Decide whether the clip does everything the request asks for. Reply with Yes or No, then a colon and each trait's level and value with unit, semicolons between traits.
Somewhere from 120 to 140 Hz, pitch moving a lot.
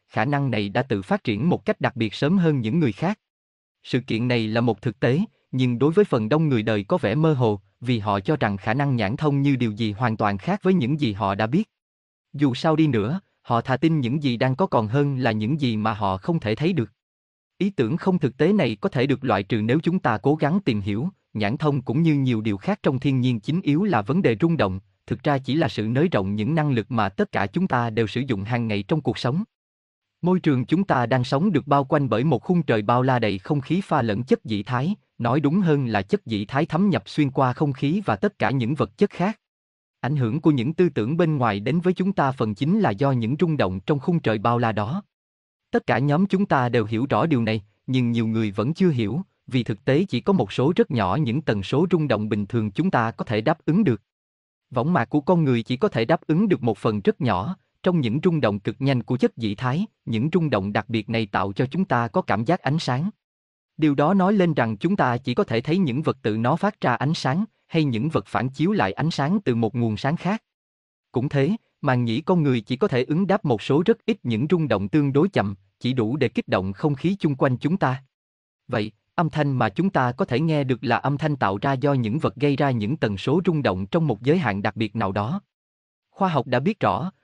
Yes: low, 135 Hz; wide, 6.2 semitones